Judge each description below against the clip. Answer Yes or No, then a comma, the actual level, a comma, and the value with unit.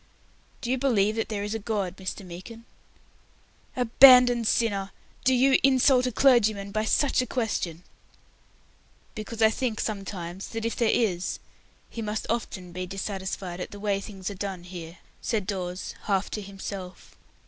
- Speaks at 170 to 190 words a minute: No, average, 160 wpm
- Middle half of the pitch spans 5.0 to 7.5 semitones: No, average, 3.5 semitones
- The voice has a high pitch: Yes, high, 210 Hz